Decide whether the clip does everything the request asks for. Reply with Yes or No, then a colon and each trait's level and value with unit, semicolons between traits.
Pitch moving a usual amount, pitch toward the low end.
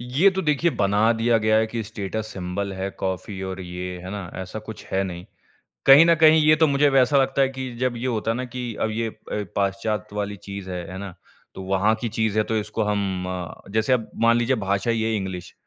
Yes: average, 3.9 semitones; low, 110 Hz